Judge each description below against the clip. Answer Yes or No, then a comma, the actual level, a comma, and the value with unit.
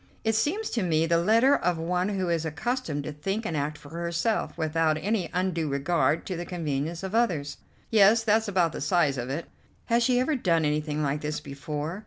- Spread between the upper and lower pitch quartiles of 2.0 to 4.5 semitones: No, wide, 5.5 semitones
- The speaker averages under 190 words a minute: No, fast, 205 wpm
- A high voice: No, medium, 170 Hz